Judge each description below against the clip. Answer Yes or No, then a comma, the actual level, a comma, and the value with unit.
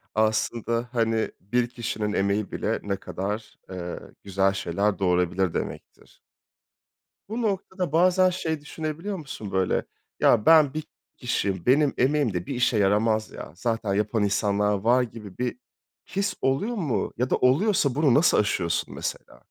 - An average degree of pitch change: No, wide, 6.7 semitones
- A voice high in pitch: No, low, 115 Hz